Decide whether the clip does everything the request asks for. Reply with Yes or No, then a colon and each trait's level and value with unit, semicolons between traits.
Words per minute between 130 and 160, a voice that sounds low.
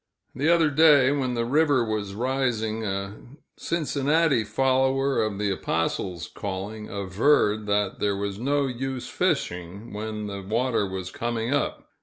Yes: average, 140 wpm; low, 115 Hz